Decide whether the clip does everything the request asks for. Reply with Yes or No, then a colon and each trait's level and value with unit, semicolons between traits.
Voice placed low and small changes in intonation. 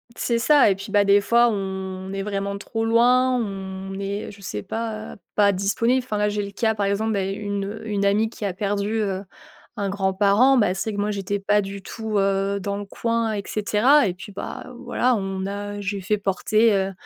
No: high, 205 Hz; narrow, 2.0 semitones